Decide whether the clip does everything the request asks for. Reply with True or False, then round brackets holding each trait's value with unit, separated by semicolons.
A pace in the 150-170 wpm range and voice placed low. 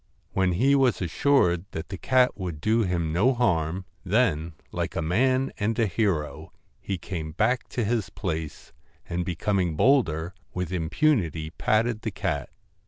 True (160 wpm; 95 Hz)